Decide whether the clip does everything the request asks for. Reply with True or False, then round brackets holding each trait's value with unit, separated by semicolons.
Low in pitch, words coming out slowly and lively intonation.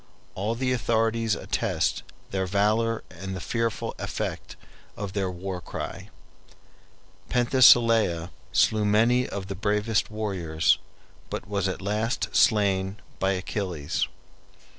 False (105 Hz; 115 wpm; 3.2 semitones)